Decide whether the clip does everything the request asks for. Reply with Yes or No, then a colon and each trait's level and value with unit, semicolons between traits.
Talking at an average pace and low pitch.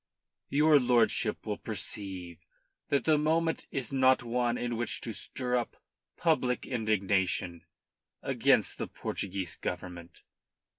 No: slow, 115 wpm; low, 120 Hz